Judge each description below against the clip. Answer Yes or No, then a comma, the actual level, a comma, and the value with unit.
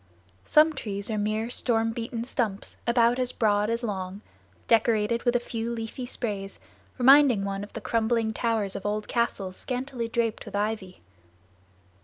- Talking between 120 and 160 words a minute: Yes, average, 155 wpm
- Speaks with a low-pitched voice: No, high, 225 Hz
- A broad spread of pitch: No, narrow, 2.5 semitones